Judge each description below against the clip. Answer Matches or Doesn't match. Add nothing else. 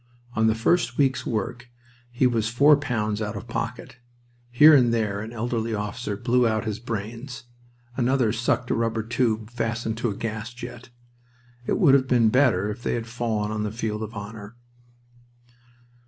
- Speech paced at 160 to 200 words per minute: Matches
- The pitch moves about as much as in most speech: Doesn't match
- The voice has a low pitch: Matches